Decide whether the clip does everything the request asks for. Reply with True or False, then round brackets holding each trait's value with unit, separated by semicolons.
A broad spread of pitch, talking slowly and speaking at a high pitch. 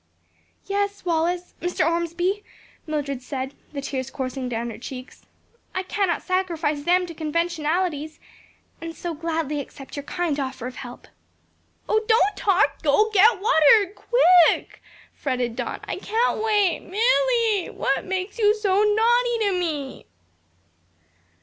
True (5.9 semitones; 130 wpm; 345 Hz)